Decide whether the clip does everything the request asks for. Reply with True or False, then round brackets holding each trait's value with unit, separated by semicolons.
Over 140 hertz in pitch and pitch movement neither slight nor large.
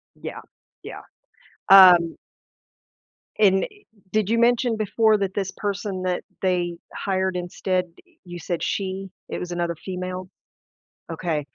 False (185 Hz; 2.1 semitones)